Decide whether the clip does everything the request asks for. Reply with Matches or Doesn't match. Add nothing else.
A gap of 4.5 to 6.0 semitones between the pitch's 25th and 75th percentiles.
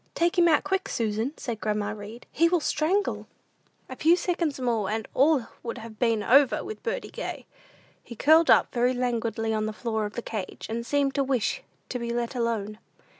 Matches